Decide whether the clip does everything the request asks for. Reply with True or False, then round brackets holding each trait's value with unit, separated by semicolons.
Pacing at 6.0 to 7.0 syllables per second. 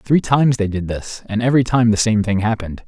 True (6.3 syllables/s)